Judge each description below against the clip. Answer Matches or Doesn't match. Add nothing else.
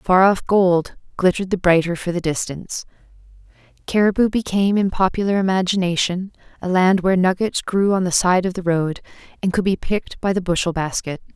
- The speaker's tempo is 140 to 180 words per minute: Matches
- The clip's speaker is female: Matches